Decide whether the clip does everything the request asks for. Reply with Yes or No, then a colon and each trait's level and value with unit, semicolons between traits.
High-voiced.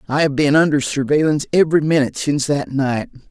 No: medium, 145 Hz